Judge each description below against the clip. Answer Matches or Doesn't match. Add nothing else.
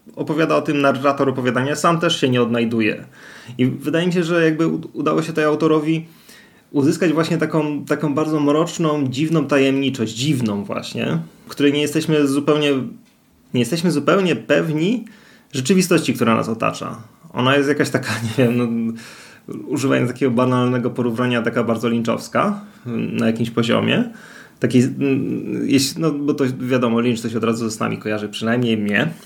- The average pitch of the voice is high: Doesn't match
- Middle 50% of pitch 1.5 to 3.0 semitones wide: Doesn't match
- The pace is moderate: Matches